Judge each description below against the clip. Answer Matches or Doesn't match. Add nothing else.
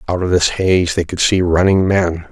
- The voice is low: Matches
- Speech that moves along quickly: Matches